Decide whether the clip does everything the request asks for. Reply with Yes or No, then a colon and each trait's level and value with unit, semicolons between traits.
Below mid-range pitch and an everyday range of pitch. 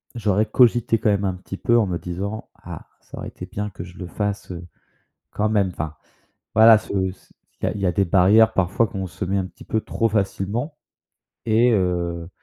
Yes: low, 100 Hz; average, 3.2 semitones